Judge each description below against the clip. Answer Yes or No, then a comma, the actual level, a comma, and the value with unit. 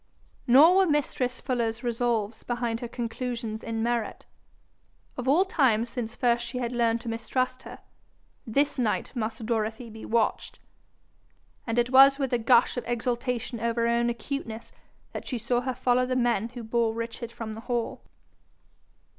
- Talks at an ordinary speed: Yes, average, 165 wpm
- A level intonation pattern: Yes, narrow, 1.7 semitones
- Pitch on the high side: Yes, high, 235 Hz